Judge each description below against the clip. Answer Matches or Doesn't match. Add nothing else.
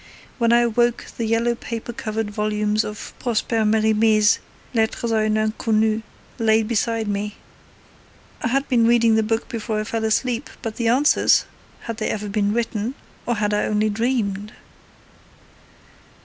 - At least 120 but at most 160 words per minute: Matches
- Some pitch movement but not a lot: Doesn't match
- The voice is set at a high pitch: Matches